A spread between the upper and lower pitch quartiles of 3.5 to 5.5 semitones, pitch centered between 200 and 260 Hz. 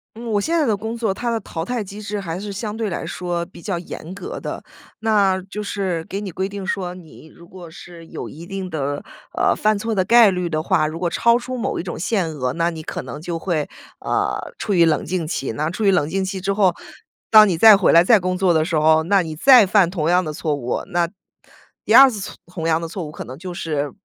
No: average, 3.9 semitones; medium, 185 Hz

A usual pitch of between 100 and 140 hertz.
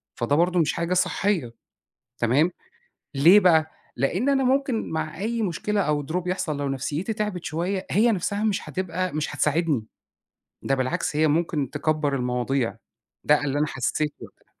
No: medium, 160 Hz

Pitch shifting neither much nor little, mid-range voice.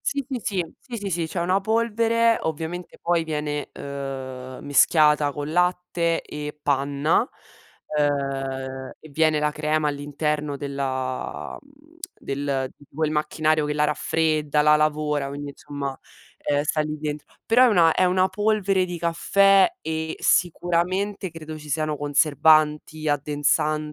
Yes: average, 3.3 semitones; medium, 155 Hz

